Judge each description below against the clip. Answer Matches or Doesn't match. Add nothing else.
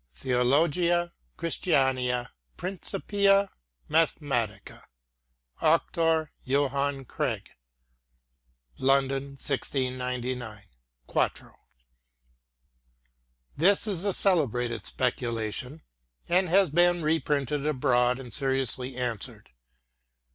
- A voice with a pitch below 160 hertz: Matches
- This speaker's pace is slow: Matches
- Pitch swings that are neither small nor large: Matches